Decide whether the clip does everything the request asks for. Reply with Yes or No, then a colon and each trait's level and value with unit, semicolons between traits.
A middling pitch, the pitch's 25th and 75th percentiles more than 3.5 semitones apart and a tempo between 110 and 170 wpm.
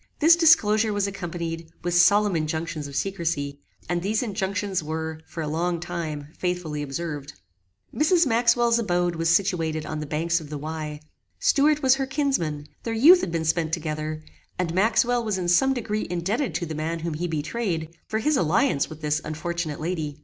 No: medium, 170 Hz; average, 5.3 semitones; average, 180 wpm